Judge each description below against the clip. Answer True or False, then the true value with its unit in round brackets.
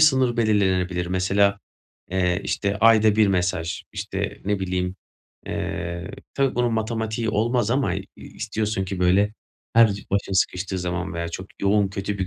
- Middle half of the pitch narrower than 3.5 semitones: True (3.1 semitones)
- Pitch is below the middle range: True (100 Hz)